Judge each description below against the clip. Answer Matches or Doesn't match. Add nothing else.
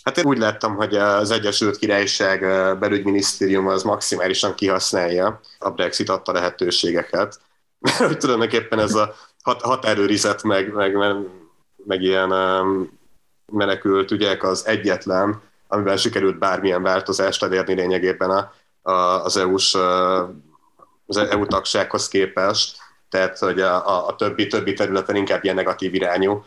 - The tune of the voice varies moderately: Doesn't match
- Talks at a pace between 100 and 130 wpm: Matches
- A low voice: Matches